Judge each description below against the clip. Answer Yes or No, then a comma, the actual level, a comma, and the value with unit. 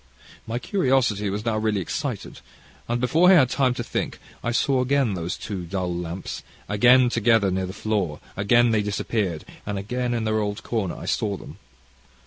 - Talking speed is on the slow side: No, average, 180 wpm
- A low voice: Yes, low, 110 Hz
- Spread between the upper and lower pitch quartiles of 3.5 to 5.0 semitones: Yes, average, 3.8 semitones